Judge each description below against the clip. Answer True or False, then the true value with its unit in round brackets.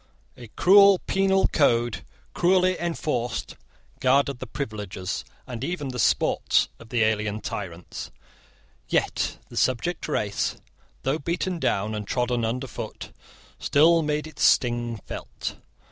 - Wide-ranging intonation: True (6.3 semitones)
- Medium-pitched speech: False (125 Hz)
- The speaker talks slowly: True (120 wpm)